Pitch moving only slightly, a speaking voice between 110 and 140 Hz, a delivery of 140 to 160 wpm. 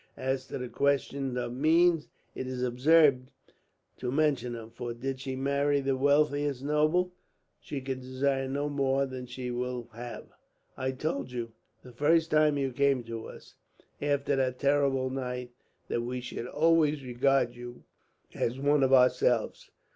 Yes: narrow, 2.3 semitones; low, 135 Hz; average, 155 wpm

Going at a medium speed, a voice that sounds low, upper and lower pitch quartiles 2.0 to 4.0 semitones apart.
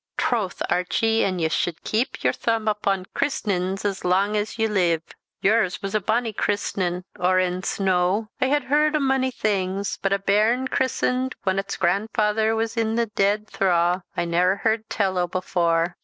No: average, 170 wpm; high, 200 Hz; average, 3.4 semitones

